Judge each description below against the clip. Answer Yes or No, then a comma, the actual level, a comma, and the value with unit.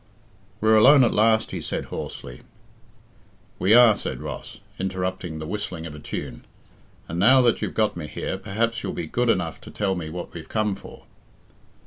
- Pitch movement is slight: No, average, 4.3 semitones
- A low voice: Yes, low, 100 Hz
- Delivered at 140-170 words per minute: No, average, 180 wpm